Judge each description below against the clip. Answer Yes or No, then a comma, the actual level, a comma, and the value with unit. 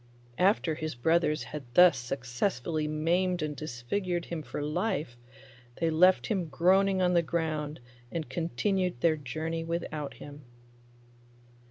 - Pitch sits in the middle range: Yes, medium, 160 Hz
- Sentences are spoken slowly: Yes, slow, 130 wpm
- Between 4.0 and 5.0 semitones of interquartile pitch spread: No, average, 3.0 semitones